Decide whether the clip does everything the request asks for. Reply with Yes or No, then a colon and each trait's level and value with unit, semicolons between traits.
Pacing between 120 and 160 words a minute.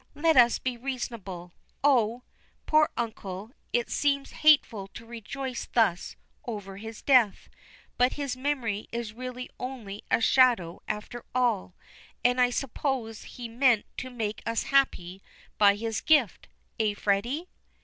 Yes: average, 140 wpm